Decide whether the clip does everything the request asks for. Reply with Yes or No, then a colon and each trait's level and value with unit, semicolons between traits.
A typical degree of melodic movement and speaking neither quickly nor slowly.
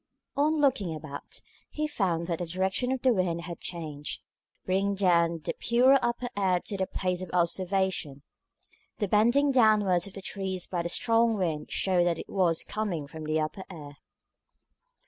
Yes: average, 4.1 semitones; average, 170 wpm